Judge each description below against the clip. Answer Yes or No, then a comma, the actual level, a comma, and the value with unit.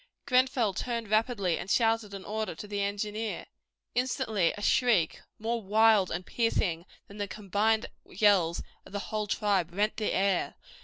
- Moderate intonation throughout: No, narrow, 2.2 semitones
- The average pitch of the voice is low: No, high, 210 Hz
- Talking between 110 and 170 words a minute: Yes, average, 155 wpm